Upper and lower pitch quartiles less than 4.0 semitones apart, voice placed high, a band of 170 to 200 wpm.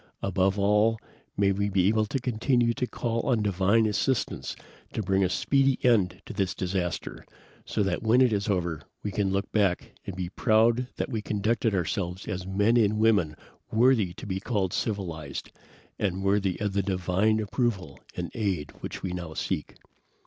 No: average, 3.1 semitones; low, 100 Hz; average, 175 wpm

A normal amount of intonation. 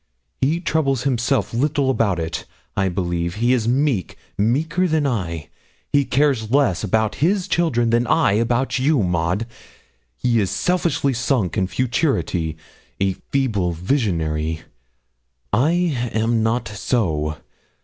No: wide, 6.6 semitones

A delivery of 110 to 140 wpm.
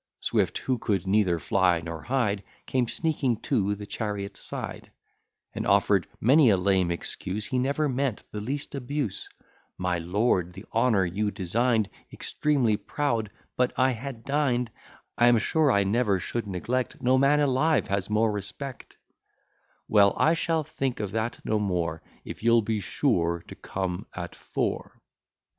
No: average, 155 wpm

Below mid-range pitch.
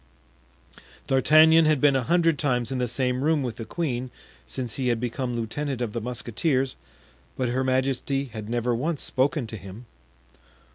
Yes: low, 130 Hz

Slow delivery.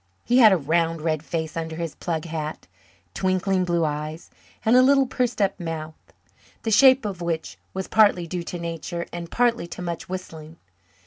No: average, 180 wpm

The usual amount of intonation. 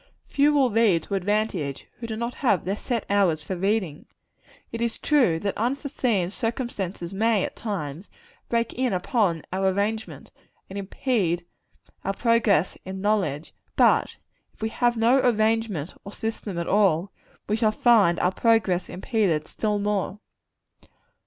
Yes: average, 3.8 semitones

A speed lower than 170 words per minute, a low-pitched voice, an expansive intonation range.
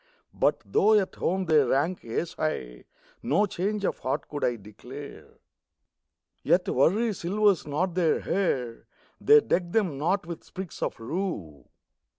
No: average, 145 wpm; medium, 170 Hz; wide, 6.3 semitones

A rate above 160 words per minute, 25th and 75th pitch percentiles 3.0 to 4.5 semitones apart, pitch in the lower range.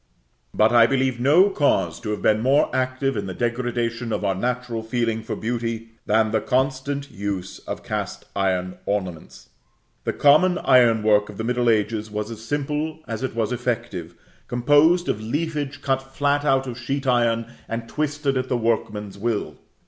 Yes: average, 170 wpm; average, 3.7 semitones; low, 120 Hz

